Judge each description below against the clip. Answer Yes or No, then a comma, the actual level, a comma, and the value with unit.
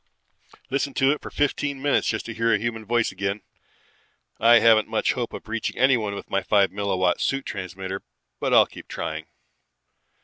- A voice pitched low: Yes, low, 110 Hz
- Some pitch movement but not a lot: Yes, average, 3.8 semitones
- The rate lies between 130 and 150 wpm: No, average, 175 wpm